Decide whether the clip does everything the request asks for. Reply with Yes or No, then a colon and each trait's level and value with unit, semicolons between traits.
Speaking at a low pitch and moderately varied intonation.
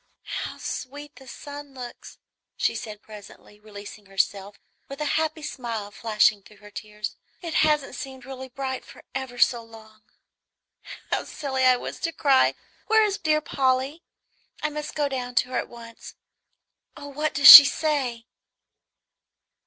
No: very high, 260 Hz; average, 4.7 semitones